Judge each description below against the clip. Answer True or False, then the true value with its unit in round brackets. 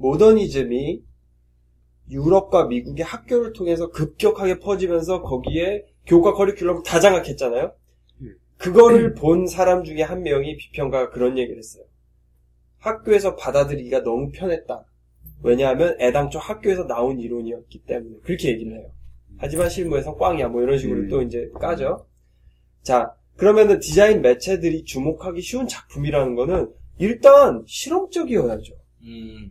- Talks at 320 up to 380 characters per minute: True (335 characters per minute)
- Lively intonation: True (7.8 semitones)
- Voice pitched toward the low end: False (150 Hz)